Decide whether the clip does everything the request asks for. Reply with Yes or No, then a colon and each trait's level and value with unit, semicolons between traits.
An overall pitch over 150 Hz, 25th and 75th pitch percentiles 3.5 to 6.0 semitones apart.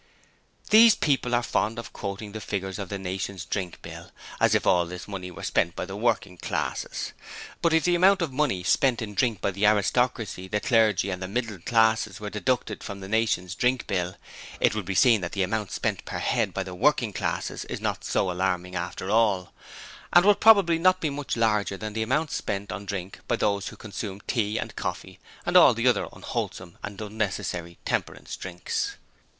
No: low, 105 Hz; average, 4.0 semitones